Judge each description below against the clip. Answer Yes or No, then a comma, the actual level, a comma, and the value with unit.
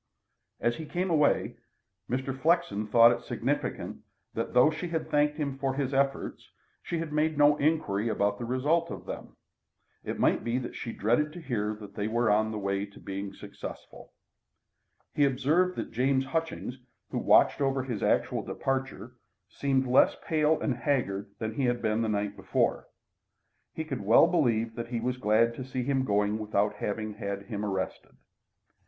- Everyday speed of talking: Yes, average, 175 wpm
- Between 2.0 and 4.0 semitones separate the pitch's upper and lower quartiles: No, average, 5.1 semitones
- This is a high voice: No, low, 125 Hz